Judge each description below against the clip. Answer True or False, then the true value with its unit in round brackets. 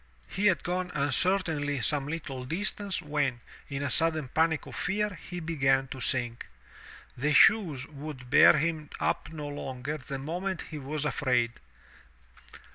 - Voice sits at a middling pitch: True (150 Hz)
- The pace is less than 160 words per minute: True (145 wpm)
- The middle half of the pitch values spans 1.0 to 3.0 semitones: False (3.7 semitones)